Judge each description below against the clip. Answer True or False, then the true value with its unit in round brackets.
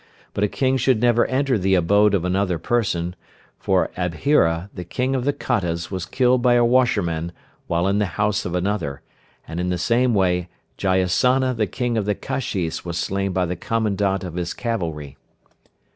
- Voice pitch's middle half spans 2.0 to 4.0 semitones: False (5.3 semitones)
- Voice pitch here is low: True (100 Hz)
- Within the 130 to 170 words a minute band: False (180 wpm)